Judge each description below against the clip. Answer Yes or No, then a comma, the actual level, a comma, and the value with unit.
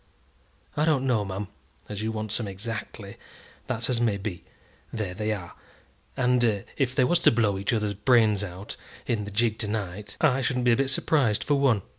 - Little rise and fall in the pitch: No, average, 3.5 semitones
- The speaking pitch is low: Yes, low, 110 Hz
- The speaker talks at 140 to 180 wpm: No, average, 195 wpm